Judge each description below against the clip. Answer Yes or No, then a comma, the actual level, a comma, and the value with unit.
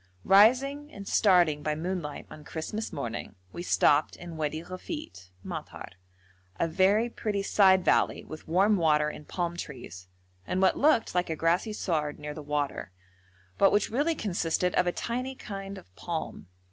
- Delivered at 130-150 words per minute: No, average, 160 wpm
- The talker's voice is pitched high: No, medium, 180 Hz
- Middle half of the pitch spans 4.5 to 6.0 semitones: Yes, average, 5.1 semitones